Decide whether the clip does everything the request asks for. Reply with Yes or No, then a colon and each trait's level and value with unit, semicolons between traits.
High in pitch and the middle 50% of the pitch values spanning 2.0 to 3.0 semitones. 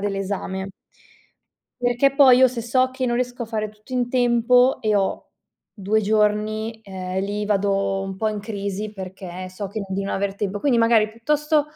No: high, 215 Hz; average, 3.6 semitones